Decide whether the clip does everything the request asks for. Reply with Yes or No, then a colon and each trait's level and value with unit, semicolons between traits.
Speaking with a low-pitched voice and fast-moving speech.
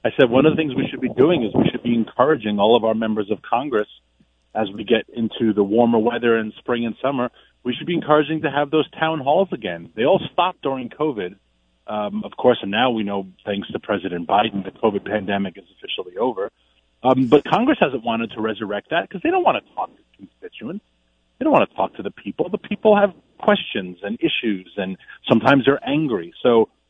Yes: low, 120 Hz; fast, 220 wpm